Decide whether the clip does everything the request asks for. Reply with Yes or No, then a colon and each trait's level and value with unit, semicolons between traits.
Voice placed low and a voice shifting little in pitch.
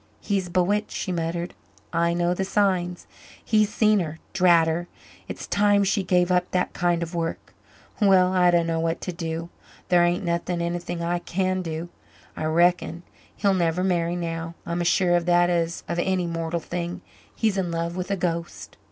No: medium, 175 Hz; narrow, 1.5 semitones